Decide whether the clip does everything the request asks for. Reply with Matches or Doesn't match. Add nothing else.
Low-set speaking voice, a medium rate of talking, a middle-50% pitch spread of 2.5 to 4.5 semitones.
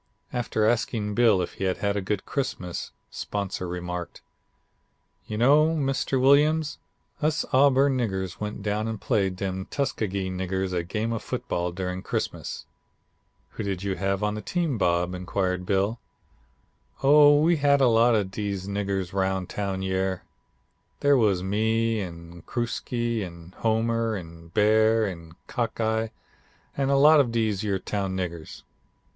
Matches